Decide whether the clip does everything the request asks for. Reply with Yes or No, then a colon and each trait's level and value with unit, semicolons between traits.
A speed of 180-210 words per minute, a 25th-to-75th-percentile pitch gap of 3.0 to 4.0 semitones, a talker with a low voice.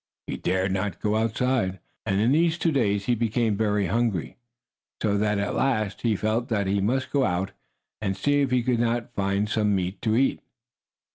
Yes: average, 195 wpm; average, 3.3 semitones; low, 110 Hz